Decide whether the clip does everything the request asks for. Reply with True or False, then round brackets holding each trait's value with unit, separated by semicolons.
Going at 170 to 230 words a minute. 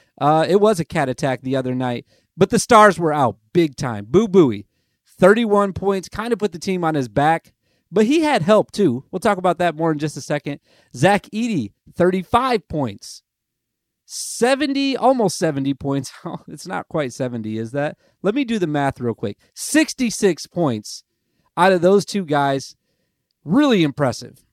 True (175 wpm)